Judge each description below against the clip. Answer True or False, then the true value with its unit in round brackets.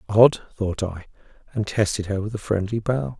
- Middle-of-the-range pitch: False (105 Hz)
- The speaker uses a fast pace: False (190 wpm)